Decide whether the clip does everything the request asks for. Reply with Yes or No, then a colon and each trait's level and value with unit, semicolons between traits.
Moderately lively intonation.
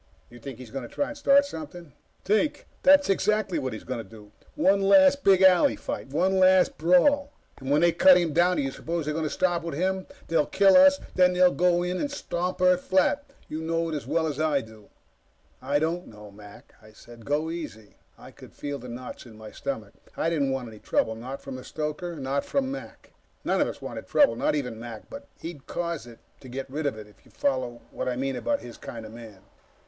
No: wide, 6.3 semitones